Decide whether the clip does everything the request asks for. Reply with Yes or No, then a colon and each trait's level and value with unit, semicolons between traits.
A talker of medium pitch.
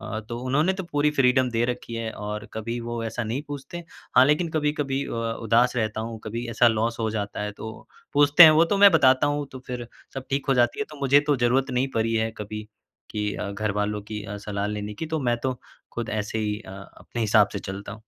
No: low, 120 Hz